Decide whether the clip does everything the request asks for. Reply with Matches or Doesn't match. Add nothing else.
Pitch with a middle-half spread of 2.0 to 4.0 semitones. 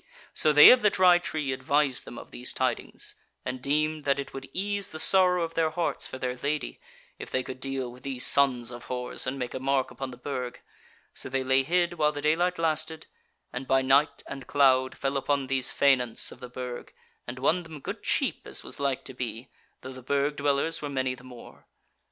Matches